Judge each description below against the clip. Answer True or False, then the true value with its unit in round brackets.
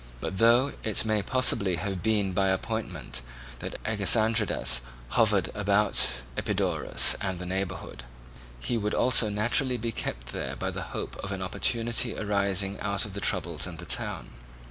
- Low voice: True (100 Hz)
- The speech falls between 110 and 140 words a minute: False (155 wpm)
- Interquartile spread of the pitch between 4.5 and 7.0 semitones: False (2.9 semitones)